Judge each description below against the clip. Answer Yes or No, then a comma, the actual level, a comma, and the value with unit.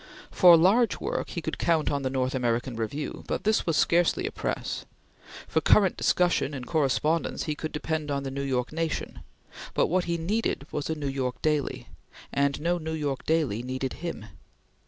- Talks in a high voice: No, medium, 150 Hz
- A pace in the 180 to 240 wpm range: Yes, average, 185 wpm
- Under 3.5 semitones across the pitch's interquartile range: No, average, 3.8 semitones